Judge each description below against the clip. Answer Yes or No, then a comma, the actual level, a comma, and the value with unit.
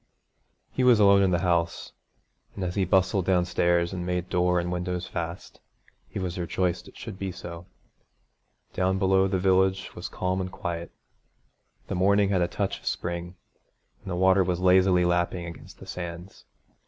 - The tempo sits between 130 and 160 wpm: No, average, 170 wpm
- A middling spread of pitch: No, narrow, 1.5 semitones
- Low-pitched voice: Yes, very low, 90 Hz